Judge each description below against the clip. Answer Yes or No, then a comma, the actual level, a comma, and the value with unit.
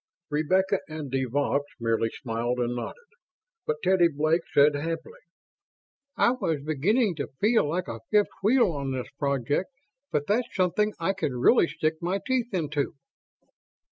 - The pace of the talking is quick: No, average, 150 wpm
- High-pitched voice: No, medium, 155 Hz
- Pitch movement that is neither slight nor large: No, wide, 6.0 semitones